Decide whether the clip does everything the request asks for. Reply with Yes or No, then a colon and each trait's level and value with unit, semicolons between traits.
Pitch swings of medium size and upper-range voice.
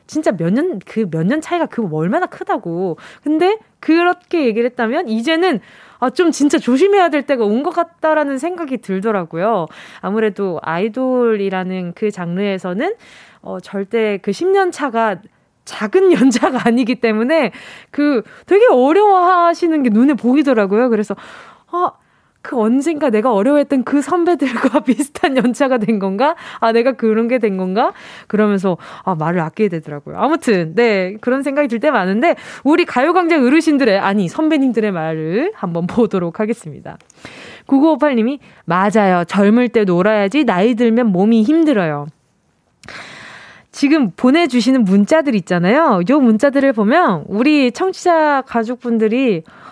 No: wide, 6.8 semitones; high, 240 Hz